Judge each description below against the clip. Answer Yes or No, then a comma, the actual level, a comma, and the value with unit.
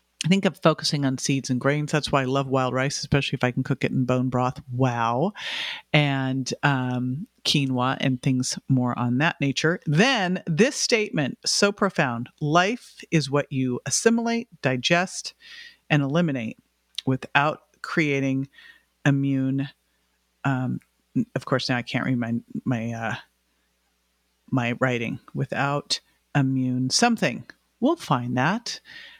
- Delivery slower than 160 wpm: Yes, average, 140 wpm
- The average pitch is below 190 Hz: Yes, low, 135 Hz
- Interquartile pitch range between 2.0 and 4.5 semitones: No, average, 5.2 semitones